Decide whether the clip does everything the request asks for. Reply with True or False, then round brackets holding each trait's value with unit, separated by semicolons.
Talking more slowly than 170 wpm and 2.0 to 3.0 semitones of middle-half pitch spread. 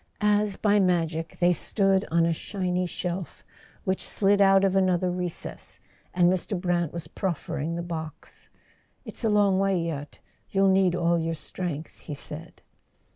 True (155 wpm; 2.5 semitones)